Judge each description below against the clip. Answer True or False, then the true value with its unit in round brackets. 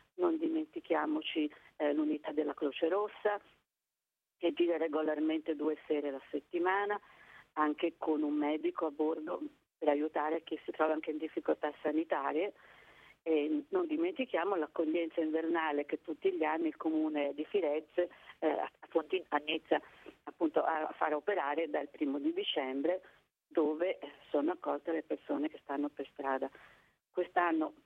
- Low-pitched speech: False (160 Hz)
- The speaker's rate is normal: True (140 wpm)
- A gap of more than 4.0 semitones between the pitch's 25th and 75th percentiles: False (2.8 semitones)